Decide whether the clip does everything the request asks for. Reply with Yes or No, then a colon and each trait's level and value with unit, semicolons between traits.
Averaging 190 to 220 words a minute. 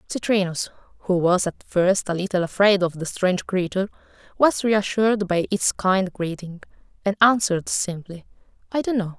No: average, 155 wpm